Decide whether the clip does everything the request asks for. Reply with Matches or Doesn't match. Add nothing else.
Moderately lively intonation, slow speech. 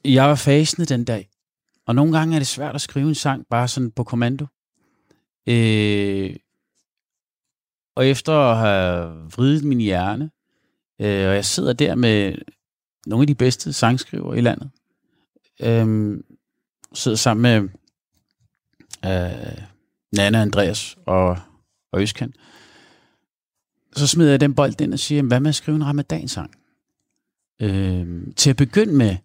Doesn't match